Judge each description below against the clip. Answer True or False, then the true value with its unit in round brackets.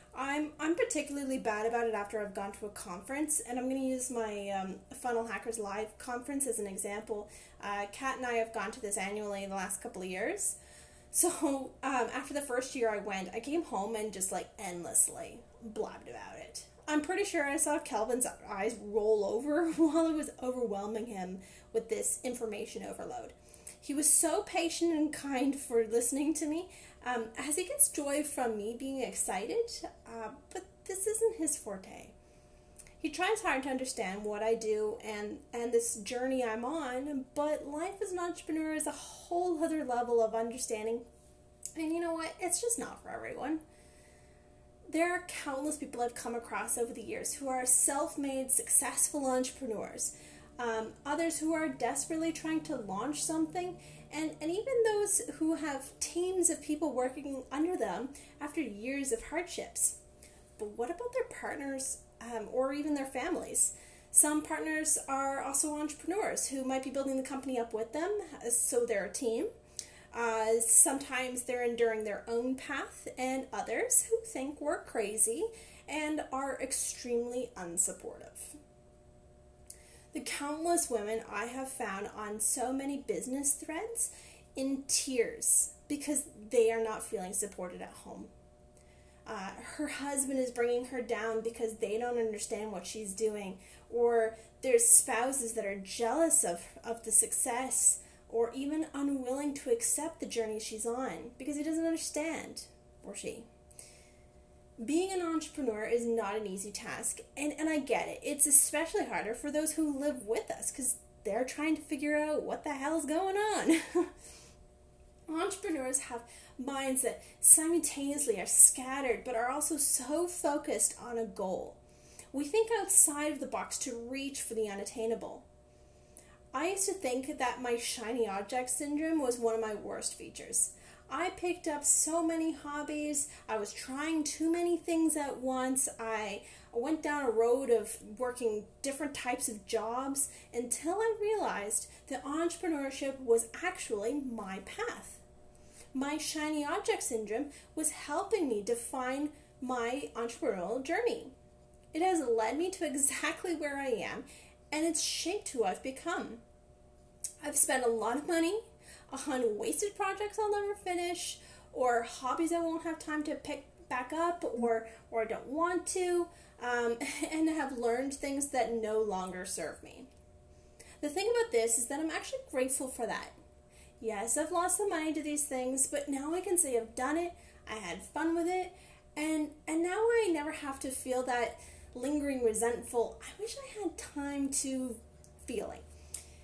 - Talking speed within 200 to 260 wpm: False (165 wpm)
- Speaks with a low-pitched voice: False (270 Hz)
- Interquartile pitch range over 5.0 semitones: True (5.5 semitones)